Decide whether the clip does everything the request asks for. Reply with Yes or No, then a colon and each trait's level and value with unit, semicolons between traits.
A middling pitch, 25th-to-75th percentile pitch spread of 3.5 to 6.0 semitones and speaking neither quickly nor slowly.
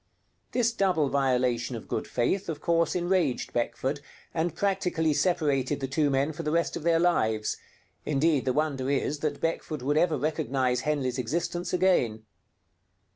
Yes: medium, 150 Hz; average, 4.2 semitones; average, 155 wpm